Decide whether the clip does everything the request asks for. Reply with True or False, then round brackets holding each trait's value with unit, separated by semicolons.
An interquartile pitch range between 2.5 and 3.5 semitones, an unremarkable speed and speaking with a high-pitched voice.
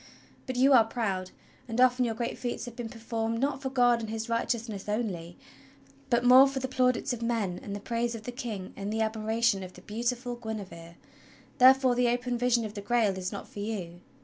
False (2.8 semitones; 210 wpm; 230 Hz)